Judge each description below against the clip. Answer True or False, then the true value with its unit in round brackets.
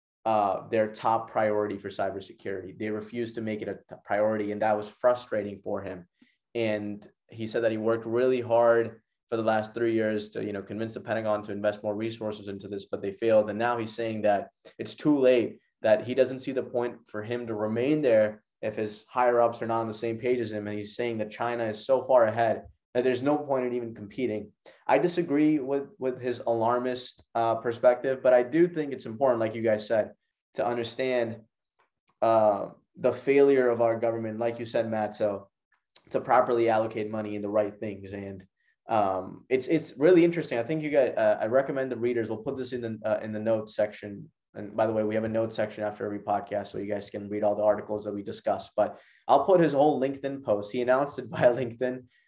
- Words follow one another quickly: True (220 wpm)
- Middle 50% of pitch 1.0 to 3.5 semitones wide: True (2.9 semitones)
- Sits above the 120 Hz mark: False (115 Hz)